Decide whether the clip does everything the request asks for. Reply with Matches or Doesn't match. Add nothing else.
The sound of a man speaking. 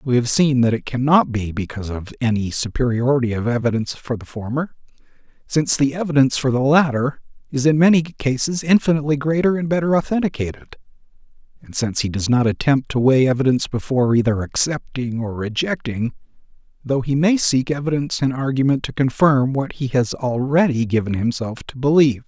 Matches